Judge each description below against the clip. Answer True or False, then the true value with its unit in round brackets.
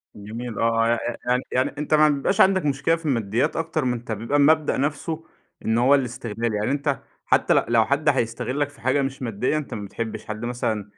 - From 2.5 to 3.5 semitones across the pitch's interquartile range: False (4.1 semitones)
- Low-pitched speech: True (130 Hz)